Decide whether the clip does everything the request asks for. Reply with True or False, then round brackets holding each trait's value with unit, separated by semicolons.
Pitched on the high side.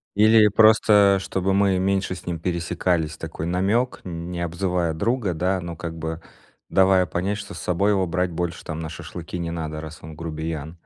False (90 Hz)